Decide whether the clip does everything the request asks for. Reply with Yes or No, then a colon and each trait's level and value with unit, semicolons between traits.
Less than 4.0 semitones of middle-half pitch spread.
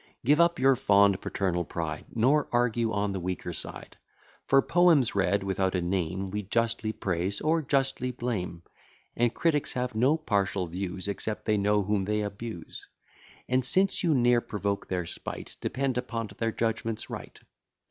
No: average, 4.5 semitones